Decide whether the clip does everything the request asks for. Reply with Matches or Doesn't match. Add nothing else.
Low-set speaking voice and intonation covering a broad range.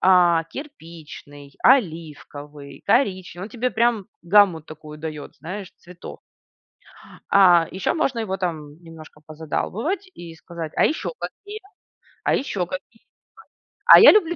Doesn't match